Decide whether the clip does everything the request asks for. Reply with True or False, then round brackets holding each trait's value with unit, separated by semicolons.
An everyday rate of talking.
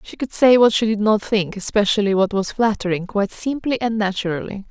True (180 wpm)